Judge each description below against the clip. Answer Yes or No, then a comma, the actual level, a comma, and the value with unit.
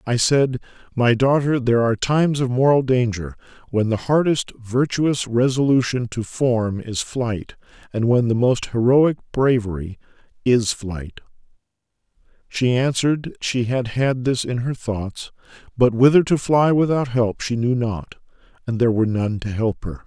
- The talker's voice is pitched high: No, low, 125 Hz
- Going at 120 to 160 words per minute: Yes, average, 155 wpm